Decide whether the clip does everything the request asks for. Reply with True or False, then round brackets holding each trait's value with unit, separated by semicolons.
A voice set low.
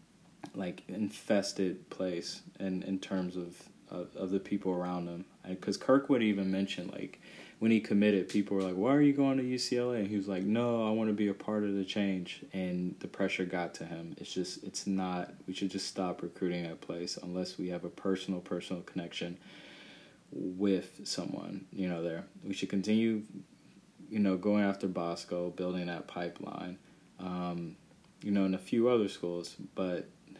True (95 Hz)